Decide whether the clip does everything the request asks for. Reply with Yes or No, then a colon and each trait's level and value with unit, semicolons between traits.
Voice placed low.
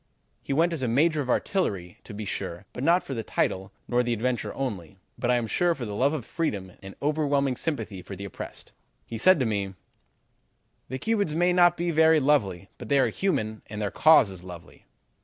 Yes: low, 125 Hz